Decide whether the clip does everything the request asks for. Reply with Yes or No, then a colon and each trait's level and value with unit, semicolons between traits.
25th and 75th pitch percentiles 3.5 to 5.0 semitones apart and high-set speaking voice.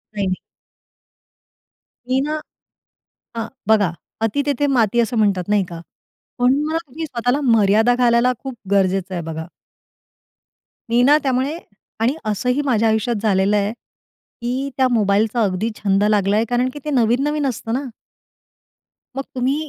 Yes: average, 4.2 semitones; high, 235 Hz